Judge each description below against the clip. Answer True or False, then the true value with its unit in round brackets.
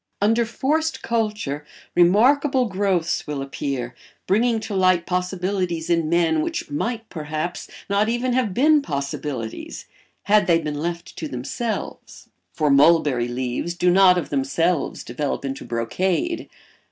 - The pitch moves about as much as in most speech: False (6.4 semitones)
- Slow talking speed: True (130 wpm)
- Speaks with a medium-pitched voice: True (175 Hz)